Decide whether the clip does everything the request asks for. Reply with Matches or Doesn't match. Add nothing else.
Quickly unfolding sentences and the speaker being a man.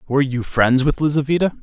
Doesn't match